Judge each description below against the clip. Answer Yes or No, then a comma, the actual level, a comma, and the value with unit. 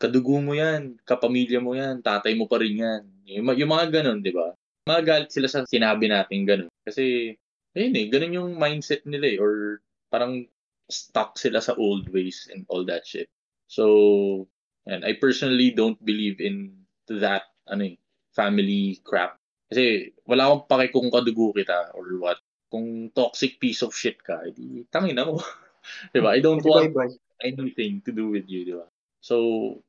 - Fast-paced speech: No, average, 175 wpm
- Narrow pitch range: No, average, 5.1 semitones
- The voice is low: Yes, low, 115 Hz